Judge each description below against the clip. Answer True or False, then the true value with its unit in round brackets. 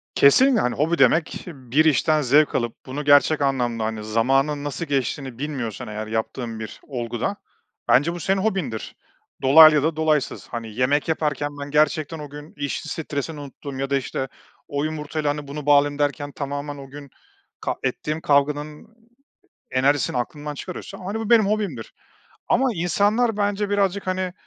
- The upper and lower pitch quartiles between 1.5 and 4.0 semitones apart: True (3.1 semitones)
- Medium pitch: True (145 Hz)